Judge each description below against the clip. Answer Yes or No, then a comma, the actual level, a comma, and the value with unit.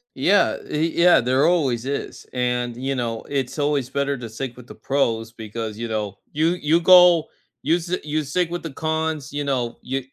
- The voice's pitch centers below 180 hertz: Yes, medium, 140 Hz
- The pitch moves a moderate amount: Yes, average, 4.7 semitones